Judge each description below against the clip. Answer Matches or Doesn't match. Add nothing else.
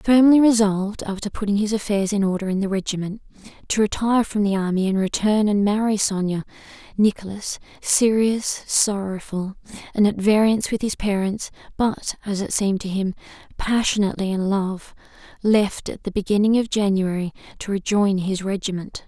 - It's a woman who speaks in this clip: Matches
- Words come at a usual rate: Matches